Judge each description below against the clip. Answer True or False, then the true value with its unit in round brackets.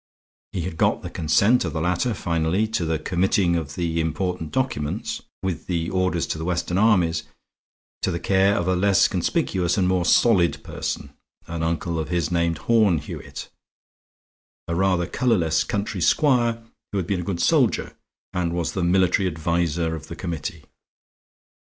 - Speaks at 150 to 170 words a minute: True (165 wpm)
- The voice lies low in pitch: True (85 Hz)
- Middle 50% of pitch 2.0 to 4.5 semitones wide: True (2.6 semitones)